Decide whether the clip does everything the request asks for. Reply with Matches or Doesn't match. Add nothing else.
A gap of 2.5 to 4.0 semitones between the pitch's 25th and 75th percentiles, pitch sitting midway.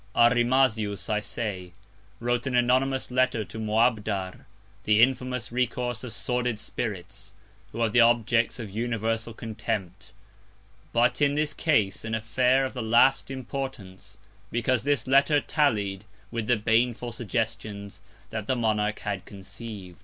Doesn't match